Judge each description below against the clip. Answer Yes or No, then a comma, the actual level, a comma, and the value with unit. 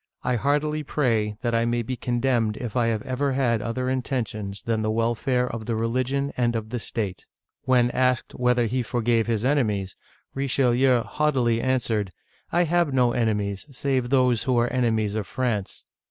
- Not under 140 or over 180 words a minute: Yes, average, 175 wpm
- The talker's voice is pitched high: No, low, 120 Hz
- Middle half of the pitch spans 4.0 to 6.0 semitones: No, narrow, 2.4 semitones